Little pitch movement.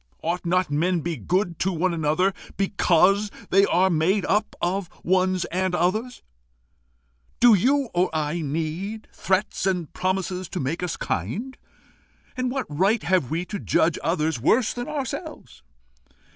No: average, 3.4 semitones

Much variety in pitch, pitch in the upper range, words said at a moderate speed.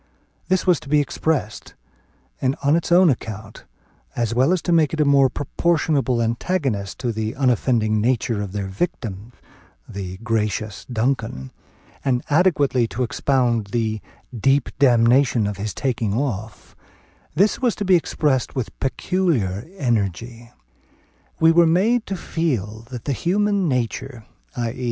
No: wide, 5.7 semitones; low, 125 Hz; average, 145 wpm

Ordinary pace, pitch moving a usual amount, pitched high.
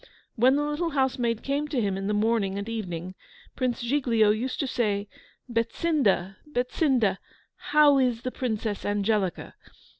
Yes: average, 145 wpm; average, 4.4 semitones; high, 230 Hz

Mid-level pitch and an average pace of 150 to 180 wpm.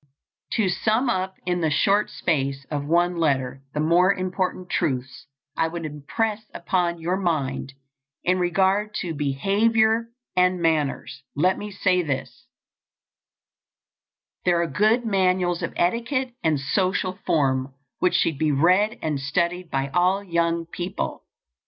No: medium, 175 Hz; slow, 135 wpm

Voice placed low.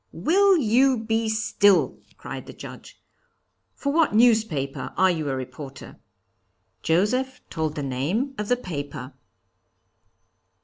No: high, 210 Hz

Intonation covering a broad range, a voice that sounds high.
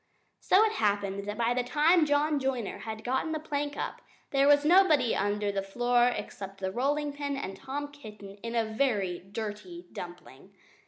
Yes: wide, 6.2 semitones; high, 240 Hz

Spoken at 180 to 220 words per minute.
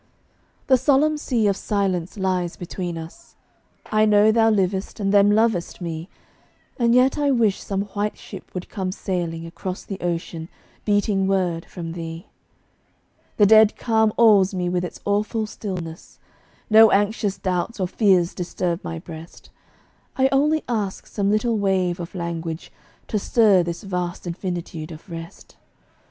No: average, 150 wpm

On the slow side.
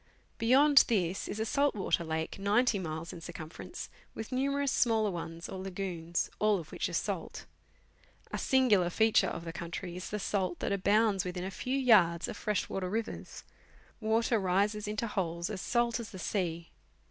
No: average, 175 wpm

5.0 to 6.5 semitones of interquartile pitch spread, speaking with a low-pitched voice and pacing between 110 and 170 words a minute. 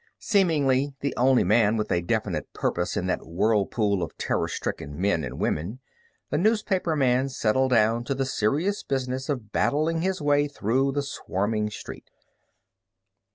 Yes: wide, 5.4 semitones; low, 125 Hz; average, 150 wpm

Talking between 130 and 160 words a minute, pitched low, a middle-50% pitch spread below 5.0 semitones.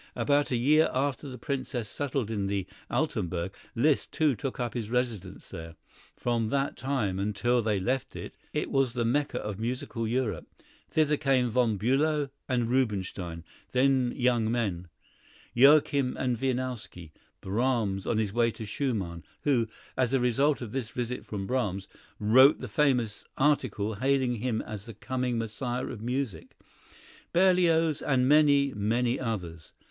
Yes: average, 150 wpm; low, 125 Hz; average, 3.9 semitones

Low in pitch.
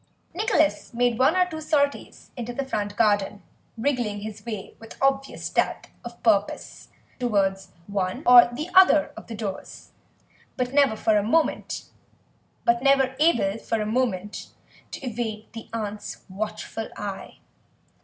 No: high, 230 Hz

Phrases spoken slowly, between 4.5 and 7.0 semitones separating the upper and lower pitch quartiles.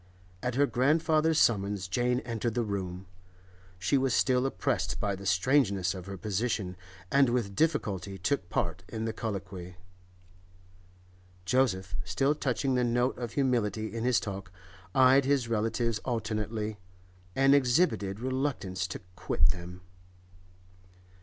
Yes: slow, 130 wpm; average, 5.1 semitones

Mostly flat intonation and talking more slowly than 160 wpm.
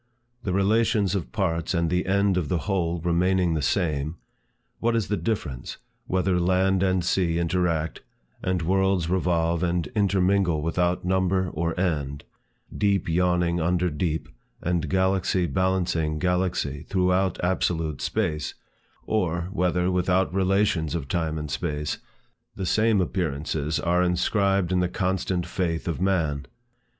Yes: narrow, 2.3 semitones; slow, 135 wpm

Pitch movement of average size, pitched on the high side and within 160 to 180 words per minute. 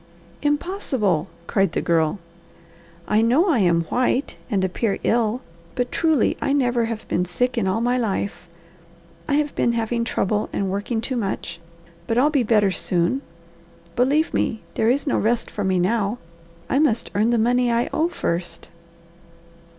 Yes: average, 4.3 semitones; high, 230 Hz; average, 165 wpm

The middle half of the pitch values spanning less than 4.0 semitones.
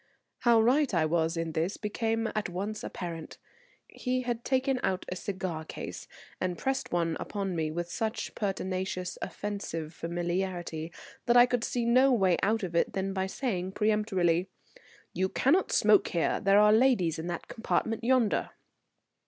No: average, 4.7 semitones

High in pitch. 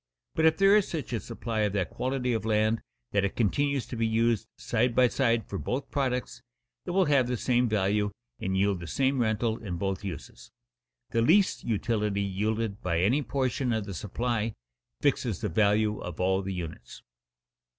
No: low, 110 Hz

